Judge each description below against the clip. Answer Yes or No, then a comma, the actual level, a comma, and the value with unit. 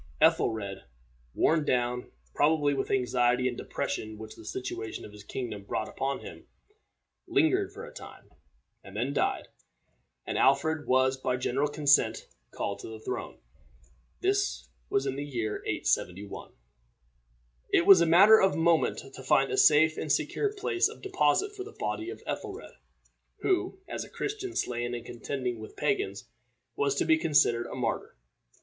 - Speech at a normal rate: Yes, average, 160 wpm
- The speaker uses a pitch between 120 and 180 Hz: Yes, medium, 140 Hz